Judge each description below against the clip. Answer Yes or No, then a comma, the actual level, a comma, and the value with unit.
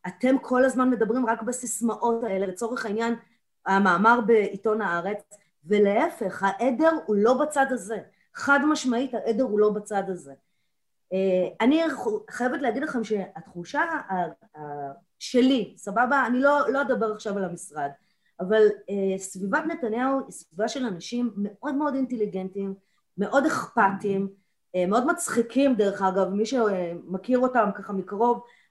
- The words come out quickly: No, average, 125 wpm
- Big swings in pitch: No, average, 4.5 semitones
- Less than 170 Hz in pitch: No, high, 220 Hz